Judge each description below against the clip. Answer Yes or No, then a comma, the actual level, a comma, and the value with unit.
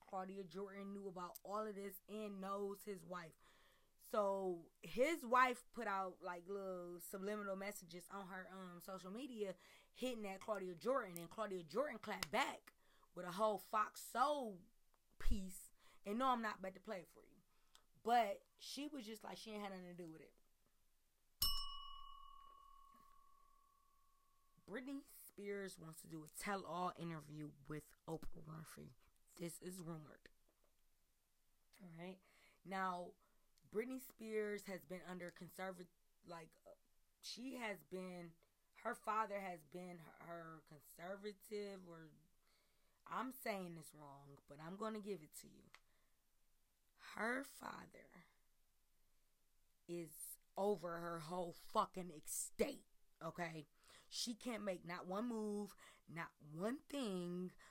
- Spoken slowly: Yes, slow, 130 wpm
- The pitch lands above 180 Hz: Yes, high, 190 Hz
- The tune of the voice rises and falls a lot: No, average, 4.0 semitones